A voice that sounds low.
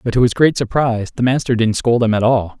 Yes: low, 115 Hz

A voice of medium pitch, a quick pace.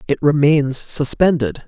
No: medium, 145 Hz; slow, 105 wpm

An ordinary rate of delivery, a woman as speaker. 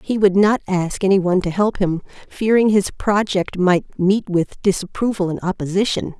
Yes: average, 175 wpm; female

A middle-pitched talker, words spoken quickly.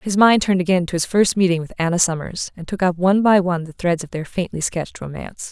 Yes: medium, 180 Hz; fast, 260 wpm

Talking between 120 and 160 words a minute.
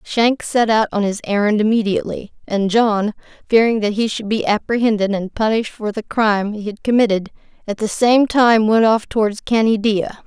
No: average, 175 wpm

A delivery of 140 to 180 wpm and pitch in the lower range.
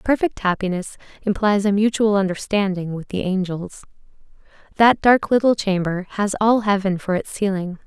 No: average, 145 wpm; high, 200 Hz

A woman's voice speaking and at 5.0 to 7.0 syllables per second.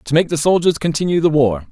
No: male; 6.3 syllables/s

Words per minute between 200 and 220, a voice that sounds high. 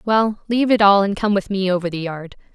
No: fast, 260 wpm; high, 200 Hz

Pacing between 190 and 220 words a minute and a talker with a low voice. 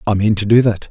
No: fast, 330 wpm; low, 105 Hz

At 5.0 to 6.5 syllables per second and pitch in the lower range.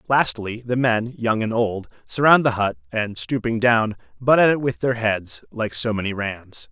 No: 4.4 syllables/s; low, 115 Hz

